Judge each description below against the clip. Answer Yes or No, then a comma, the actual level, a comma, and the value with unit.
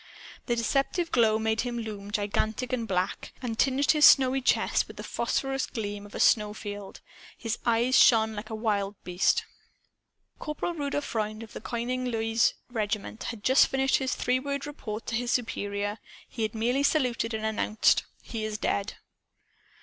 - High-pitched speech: Yes, high, 225 Hz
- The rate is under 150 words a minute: No, average, 165 wpm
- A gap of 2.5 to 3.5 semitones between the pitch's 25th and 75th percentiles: Yes, average, 3.1 semitones